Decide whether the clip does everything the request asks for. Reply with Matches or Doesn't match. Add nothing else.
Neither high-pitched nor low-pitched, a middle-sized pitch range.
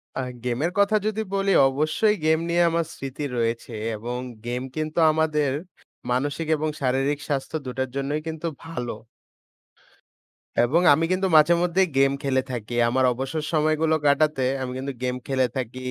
Matches